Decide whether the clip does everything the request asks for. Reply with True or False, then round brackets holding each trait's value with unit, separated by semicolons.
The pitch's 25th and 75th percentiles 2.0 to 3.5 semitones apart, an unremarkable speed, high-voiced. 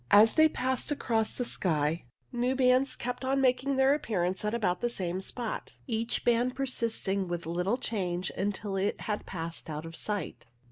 False (5.6 semitones; 175 wpm; 220 Hz)